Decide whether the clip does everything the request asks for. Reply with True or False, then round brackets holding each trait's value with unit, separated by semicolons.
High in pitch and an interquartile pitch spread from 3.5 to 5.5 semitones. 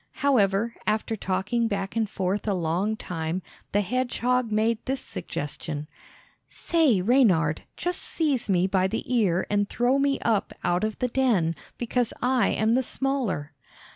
True (215 Hz; 5.1 semitones)